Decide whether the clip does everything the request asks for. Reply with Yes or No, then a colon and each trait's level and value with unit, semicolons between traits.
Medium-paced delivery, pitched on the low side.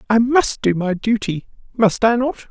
No: average, 190 wpm; high, 225 Hz